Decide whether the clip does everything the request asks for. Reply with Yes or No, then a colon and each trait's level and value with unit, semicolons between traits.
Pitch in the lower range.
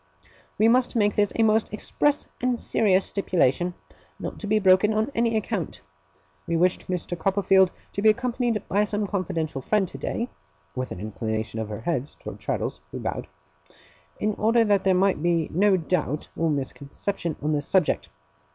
No: high, 190 Hz